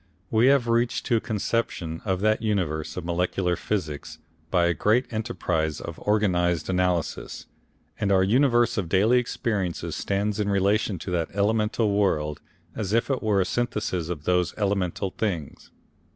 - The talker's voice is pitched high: No, low, 100 Hz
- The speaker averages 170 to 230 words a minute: No, average, 155 wpm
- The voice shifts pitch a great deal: No, average, 3.8 semitones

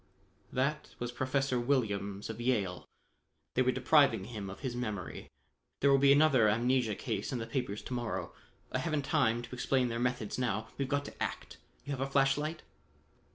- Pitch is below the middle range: Yes, low, 125 Hz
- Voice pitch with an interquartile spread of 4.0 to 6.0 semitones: No, average, 3.4 semitones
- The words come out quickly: No, average, 185 wpm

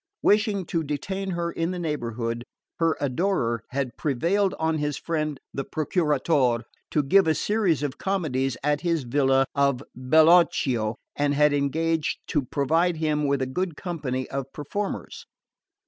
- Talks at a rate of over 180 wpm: No, average, 145 wpm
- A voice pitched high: No, medium, 150 Hz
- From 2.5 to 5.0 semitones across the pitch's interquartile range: Yes, average, 3.9 semitones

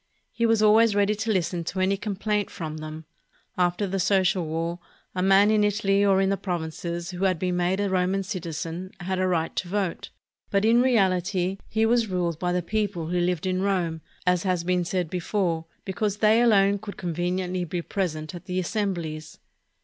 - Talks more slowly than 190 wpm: No, average, 195 wpm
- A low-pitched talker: No, medium, 185 Hz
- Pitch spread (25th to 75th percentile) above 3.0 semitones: No, narrow, 2.5 semitones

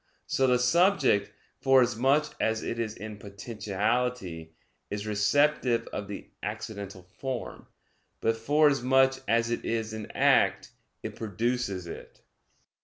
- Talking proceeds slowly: Yes, slow, 115 wpm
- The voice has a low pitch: Yes, low, 115 Hz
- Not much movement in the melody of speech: No, average, 3.7 semitones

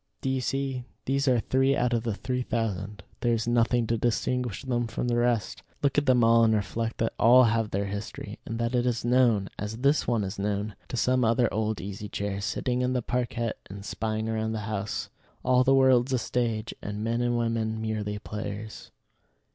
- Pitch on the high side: No, low, 115 Hz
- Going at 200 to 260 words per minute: Yes, fast, 205 wpm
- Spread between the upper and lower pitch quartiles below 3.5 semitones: Yes, narrow, 2.5 semitones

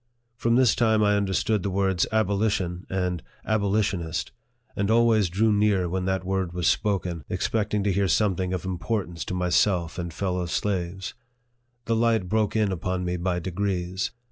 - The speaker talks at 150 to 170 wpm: Yes, average, 165 wpm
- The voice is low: Yes, very low, 95 Hz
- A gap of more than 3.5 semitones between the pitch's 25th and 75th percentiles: No, average, 2.9 semitones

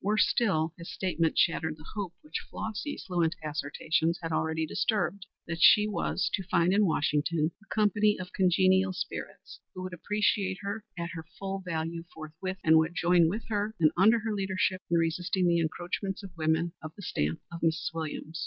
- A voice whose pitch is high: No, medium, 175 Hz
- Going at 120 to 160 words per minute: No, average, 180 wpm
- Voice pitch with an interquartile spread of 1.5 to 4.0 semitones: Yes, average, 3.3 semitones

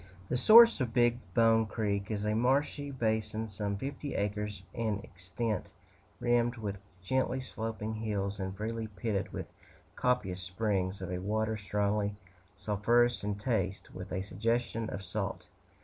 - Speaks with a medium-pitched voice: No, low, 110 Hz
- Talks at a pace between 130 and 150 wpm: Yes, average, 145 wpm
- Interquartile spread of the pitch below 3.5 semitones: Yes, average, 2.7 semitones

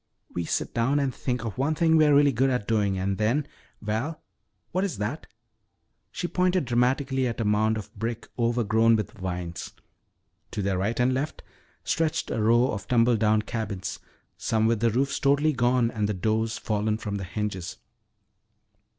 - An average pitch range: Yes, average, 3.9 semitones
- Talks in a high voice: No, low, 115 Hz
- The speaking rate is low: No, average, 175 wpm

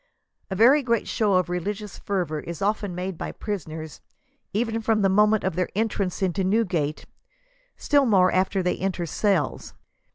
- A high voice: Yes, high, 195 Hz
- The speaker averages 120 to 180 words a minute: Yes, average, 170 wpm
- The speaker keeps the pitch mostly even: No, average, 3.0 semitones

